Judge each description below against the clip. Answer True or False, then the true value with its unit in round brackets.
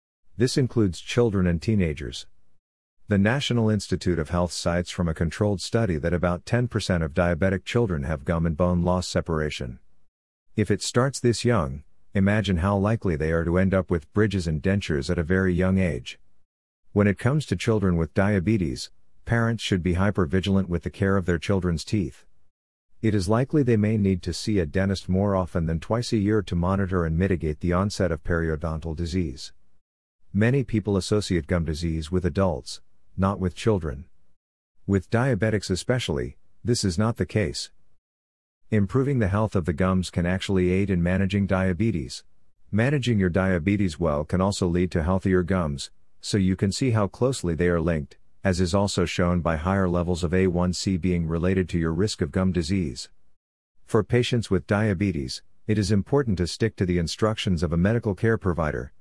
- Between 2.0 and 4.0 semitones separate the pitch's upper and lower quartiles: True (3.3 semitones)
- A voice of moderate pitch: False (95 Hz)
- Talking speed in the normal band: True (180 wpm)